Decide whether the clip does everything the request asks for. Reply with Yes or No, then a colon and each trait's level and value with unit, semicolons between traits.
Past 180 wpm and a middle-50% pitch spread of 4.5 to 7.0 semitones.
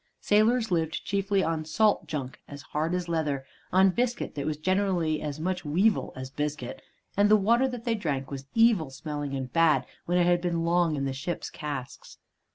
Yes: average, 190 wpm; average, 5.1 semitones